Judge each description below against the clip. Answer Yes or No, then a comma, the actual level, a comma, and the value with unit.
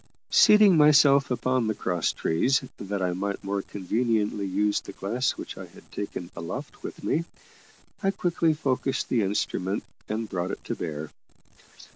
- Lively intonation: Yes, wide, 6.2 semitones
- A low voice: Yes, low, 105 Hz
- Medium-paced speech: Yes, average, 155 wpm